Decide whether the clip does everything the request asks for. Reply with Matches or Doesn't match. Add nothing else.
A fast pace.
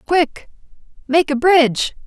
Doesn't match